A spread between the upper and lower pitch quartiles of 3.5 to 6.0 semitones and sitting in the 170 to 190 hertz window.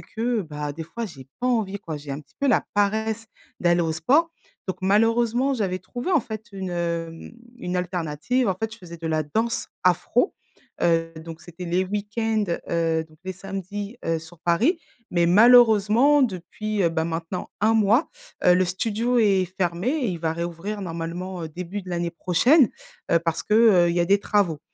Yes: average, 4.7 semitones; medium, 185 Hz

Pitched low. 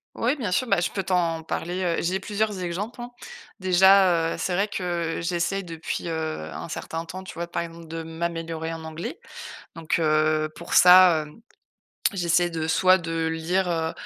No: medium, 170 Hz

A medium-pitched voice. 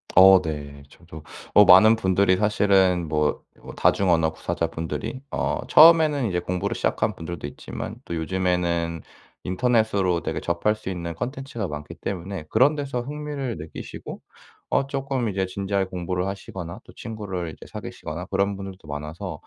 No: very low, 95 Hz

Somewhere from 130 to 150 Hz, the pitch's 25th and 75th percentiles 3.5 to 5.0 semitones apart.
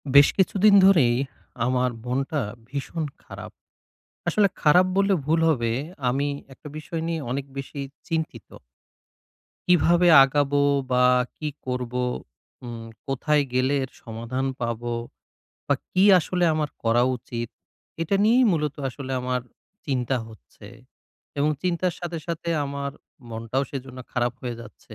Yes: medium, 140 Hz; average, 4.7 semitones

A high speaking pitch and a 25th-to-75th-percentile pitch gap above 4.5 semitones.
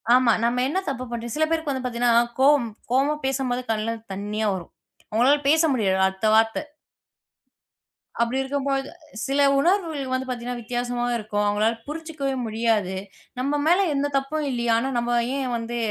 No: very high, 250 Hz; average, 3.3 semitones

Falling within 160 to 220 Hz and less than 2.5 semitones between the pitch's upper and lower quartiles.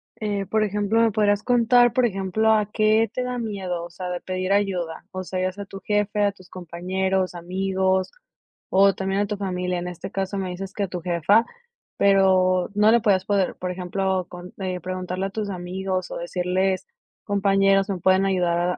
Yes: high, 190 Hz; narrow, 1.9 semitones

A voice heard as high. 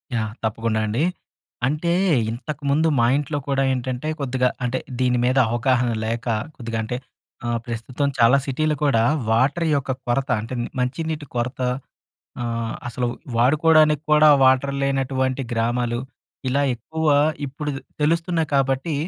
No: low, 130 Hz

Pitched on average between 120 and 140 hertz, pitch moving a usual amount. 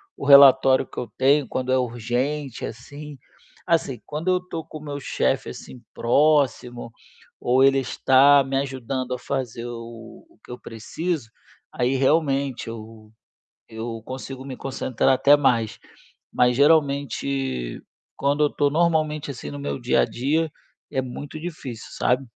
Yes: low, 135 Hz; average, 3.0 semitones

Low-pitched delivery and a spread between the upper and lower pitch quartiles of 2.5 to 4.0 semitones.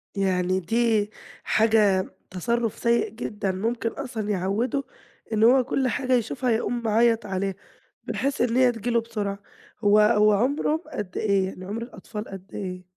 No: high, 220 Hz; average, 3.2 semitones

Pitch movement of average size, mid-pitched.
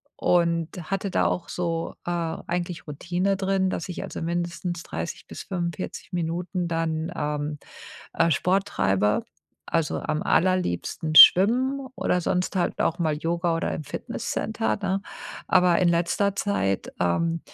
No: narrow, 2.2 semitones; medium, 170 Hz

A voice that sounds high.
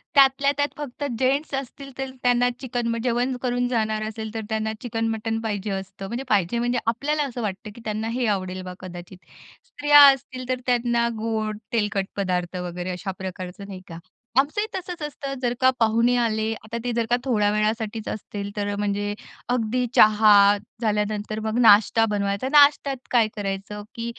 Yes: high, 225 Hz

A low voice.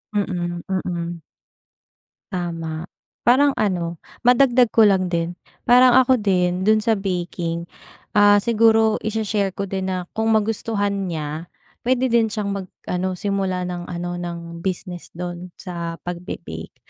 No: medium, 185 Hz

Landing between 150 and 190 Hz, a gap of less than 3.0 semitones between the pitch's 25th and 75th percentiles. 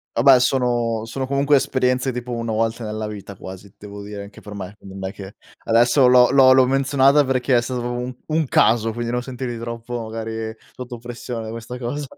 No: low, 120 Hz; narrow, 2.4 semitones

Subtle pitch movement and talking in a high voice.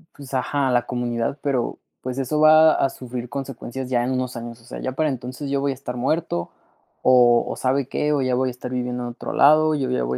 No: narrow, 2.2 semitones; low, 130 Hz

